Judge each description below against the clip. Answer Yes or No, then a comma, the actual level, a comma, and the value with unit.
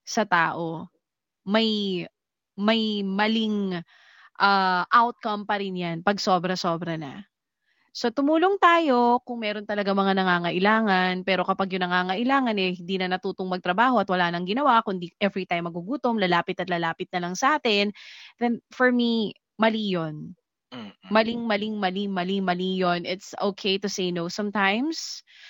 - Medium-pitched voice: No, high, 195 Hz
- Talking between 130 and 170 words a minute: Yes, average, 140 wpm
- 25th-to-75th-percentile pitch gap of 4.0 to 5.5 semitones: No, average, 3.5 semitones